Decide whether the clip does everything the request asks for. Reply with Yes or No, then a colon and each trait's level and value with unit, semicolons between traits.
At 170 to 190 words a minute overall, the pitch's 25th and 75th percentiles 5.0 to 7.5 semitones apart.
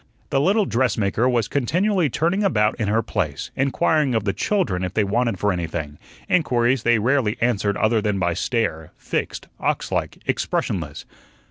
No: average, 160 wpm; wide, 5.6 semitones